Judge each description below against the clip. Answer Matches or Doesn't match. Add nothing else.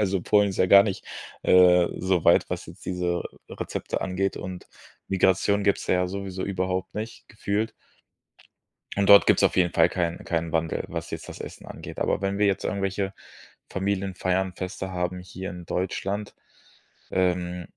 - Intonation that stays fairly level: Matches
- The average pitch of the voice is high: Doesn't match